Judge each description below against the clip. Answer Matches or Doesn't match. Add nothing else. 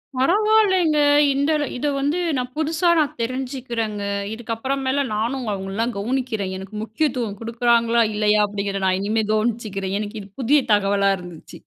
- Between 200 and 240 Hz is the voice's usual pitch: Matches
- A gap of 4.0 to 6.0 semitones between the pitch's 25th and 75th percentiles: Matches